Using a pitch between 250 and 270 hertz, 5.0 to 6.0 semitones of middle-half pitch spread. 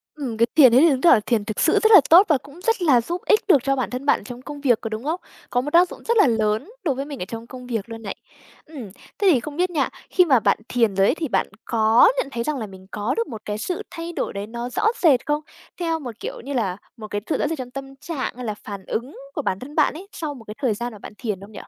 Yes: very high, 255 Hz; wide, 5.4 semitones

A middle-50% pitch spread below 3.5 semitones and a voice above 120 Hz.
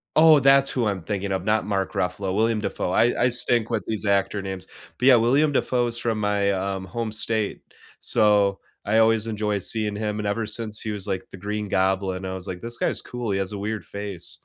No: narrow, 2.6 semitones; low, 105 Hz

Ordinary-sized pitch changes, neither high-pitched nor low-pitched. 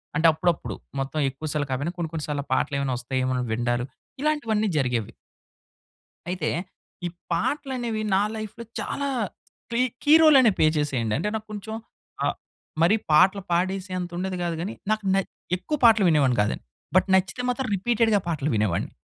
No: wide, 7.4 semitones; medium, 180 Hz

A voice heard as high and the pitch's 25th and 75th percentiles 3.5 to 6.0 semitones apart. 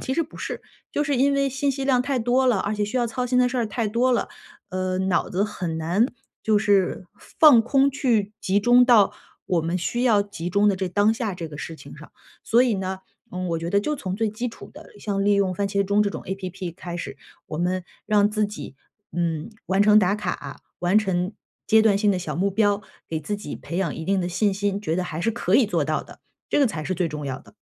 Yes: high, 205 Hz; average, 4.0 semitones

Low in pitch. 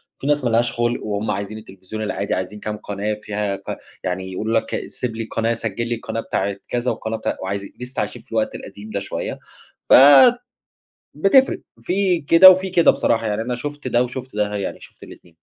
Yes: low, 110 Hz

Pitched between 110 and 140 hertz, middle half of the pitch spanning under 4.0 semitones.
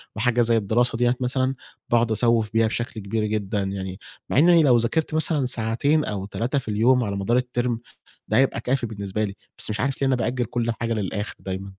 Yes: low, 115 Hz; average, 2.9 semitones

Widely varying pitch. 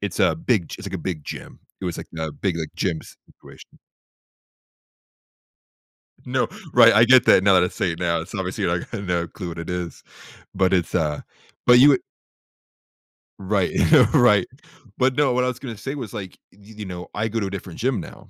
No: average, 4.7 semitones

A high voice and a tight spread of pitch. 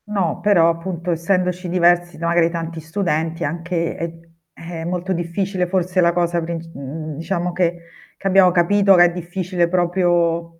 No: medium, 175 Hz; narrow, 1.5 semitones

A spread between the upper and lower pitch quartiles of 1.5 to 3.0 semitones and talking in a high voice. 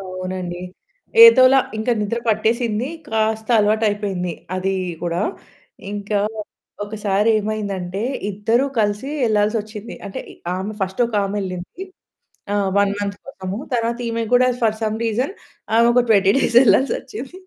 Yes: average, 2.7 semitones; high, 210 Hz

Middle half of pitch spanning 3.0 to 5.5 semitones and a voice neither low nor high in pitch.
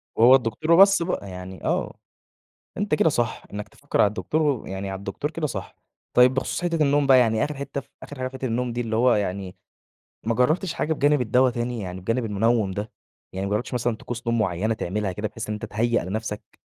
No: average, 4.5 semitones; low, 115 Hz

